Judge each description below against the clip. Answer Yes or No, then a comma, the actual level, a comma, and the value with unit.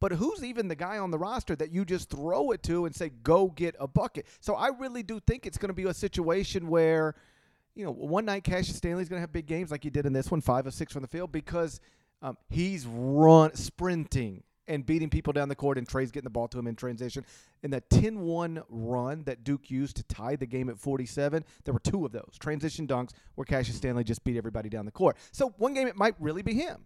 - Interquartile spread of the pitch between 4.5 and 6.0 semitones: Yes, average, 5.1 semitones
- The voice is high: No, medium, 155 Hz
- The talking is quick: Yes, fast, 250 wpm